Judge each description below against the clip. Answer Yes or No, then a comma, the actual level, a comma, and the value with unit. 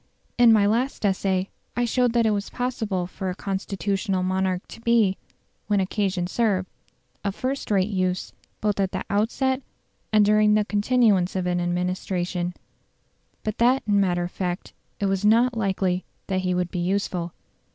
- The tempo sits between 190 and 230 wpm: No, average, 165 wpm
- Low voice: No, high, 195 Hz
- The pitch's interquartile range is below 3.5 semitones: Yes, average, 2.9 semitones